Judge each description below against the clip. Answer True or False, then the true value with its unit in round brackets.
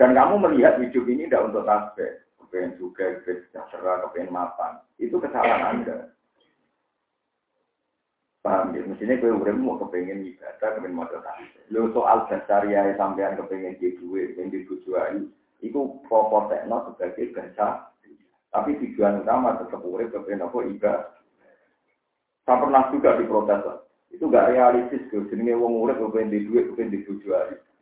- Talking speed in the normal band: False (145 wpm)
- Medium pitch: False (120 Hz)